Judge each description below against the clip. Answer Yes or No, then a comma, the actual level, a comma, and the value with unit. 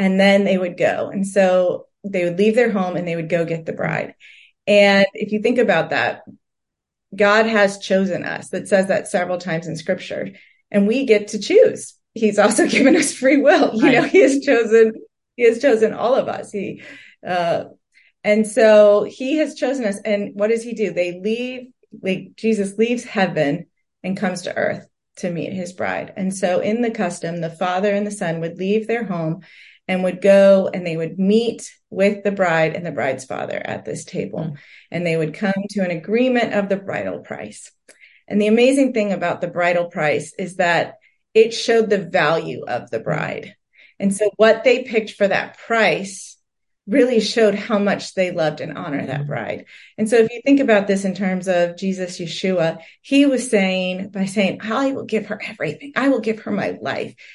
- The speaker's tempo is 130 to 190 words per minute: No, average, 200 wpm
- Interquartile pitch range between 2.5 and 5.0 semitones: Yes, average, 3.7 semitones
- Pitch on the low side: No, high, 205 Hz